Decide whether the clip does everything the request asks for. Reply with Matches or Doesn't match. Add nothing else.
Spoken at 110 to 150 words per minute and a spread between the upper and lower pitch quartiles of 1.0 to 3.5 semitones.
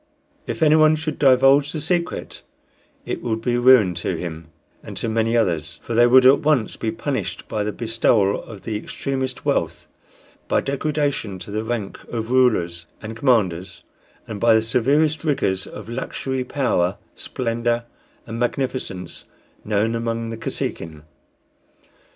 Doesn't match